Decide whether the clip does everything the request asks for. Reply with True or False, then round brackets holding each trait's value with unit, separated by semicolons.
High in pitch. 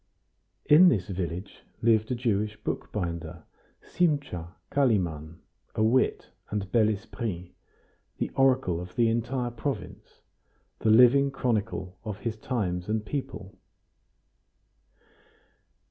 False (110 Hz)